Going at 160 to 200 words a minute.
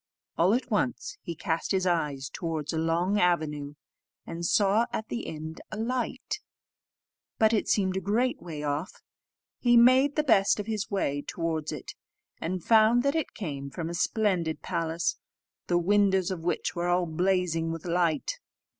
Yes: average, 165 wpm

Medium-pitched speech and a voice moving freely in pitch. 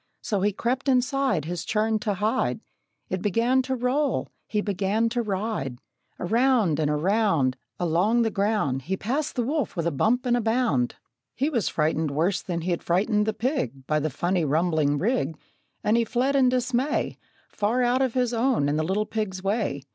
No: high, 210 Hz; wide, 6.4 semitones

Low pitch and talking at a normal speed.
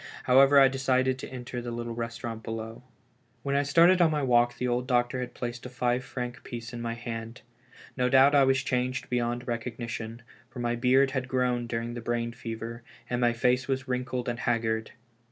Yes: low, 125 Hz; average, 195 wpm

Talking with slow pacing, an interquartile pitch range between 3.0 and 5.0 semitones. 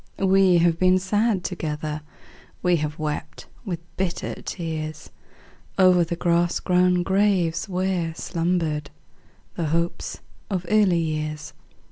No: slow, 115 wpm; narrow, 2.6 semitones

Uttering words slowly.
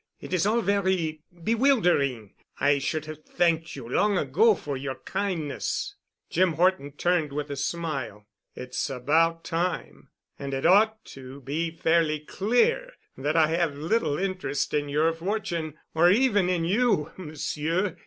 No: average, 145 wpm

